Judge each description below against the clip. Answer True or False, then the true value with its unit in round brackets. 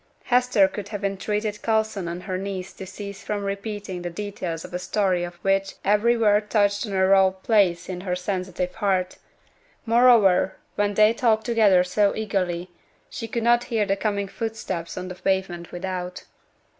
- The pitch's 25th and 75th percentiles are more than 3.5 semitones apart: False (2.6 semitones)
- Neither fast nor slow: True (170 wpm)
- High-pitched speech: True (195 Hz)